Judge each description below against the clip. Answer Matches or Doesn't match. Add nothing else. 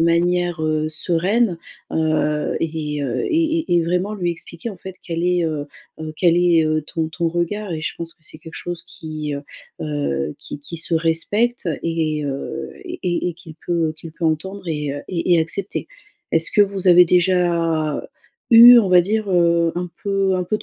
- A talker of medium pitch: Matches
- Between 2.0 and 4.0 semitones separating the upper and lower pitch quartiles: Matches